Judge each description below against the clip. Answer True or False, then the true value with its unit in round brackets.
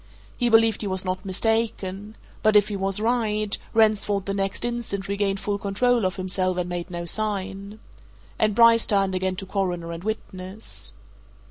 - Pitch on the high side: True (200 Hz)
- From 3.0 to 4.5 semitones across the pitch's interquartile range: False (2.5 semitones)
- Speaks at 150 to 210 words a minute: True (165 wpm)